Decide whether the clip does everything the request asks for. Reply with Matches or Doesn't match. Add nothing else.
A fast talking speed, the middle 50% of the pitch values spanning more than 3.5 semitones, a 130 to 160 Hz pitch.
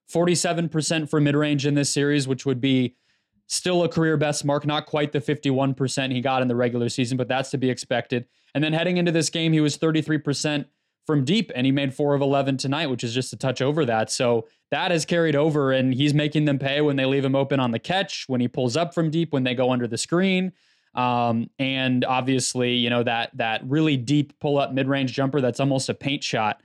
Doesn't match